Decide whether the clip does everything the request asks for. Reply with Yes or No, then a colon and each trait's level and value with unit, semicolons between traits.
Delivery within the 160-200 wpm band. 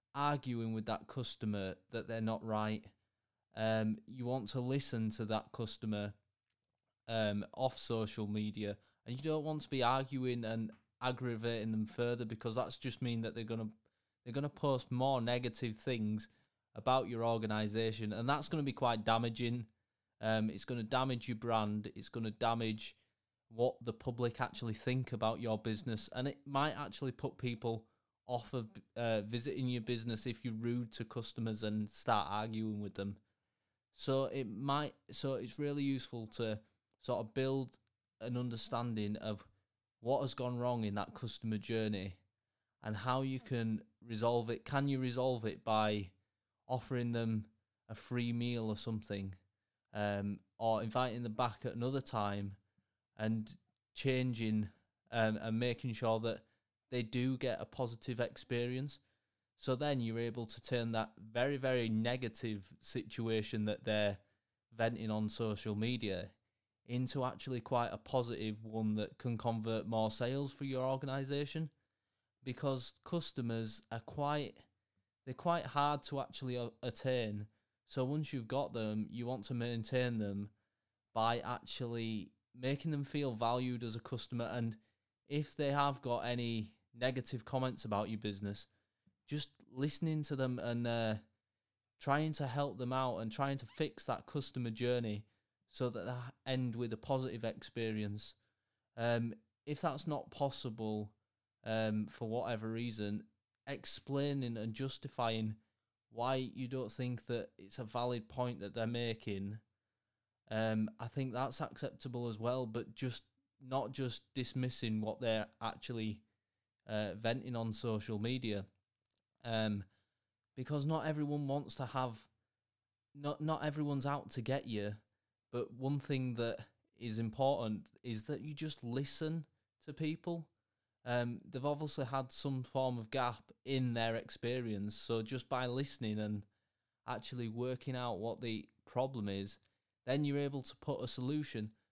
No: average, 150 wpm